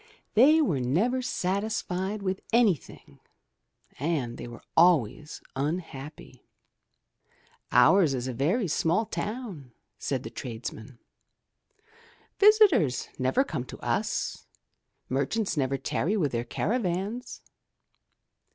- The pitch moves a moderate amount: No, wide, 8.4 semitones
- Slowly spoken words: Yes, slow, 105 wpm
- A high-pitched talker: No, medium, 170 Hz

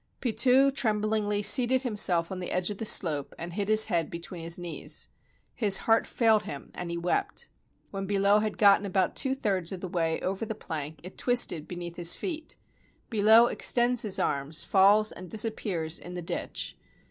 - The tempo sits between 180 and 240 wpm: Yes, average, 185 wpm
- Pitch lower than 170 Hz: No, high, 200 Hz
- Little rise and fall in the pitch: No, average, 4.1 semitones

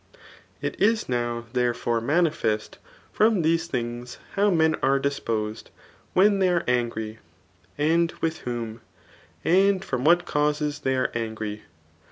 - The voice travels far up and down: Yes, wide, 6.2 semitones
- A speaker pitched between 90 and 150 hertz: Yes, medium, 140 Hz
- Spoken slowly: Yes, slow, 130 wpm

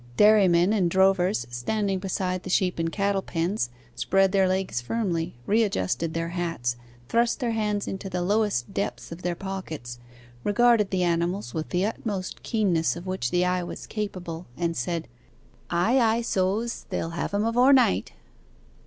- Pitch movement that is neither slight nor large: Yes, average, 3.5 semitones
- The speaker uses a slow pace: No, average, 160 wpm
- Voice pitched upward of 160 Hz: Yes, medium, 185 Hz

